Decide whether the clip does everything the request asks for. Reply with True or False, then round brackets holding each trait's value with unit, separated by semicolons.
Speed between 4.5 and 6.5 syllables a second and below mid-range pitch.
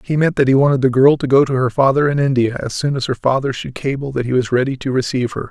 False (6.7 syllables/s; 130 Hz)